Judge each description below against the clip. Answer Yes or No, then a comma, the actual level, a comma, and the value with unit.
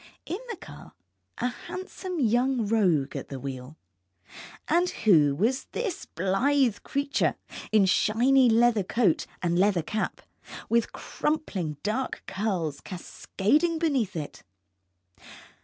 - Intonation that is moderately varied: No, wide, 7.1 semitones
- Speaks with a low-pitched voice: No, high, 220 Hz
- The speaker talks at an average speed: No, slow, 115 wpm